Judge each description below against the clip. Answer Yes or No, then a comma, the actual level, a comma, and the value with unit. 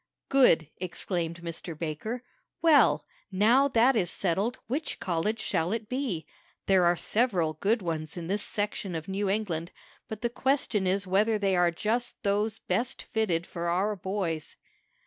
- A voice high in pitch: Yes, high, 195 Hz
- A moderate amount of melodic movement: Yes, average, 4.7 semitones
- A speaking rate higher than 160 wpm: No, average, 155 wpm